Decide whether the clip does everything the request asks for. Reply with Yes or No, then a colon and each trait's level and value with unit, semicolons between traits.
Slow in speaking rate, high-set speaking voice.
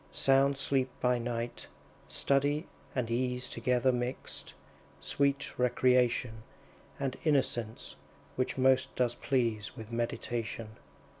No: slow, 100 wpm; low, 125 Hz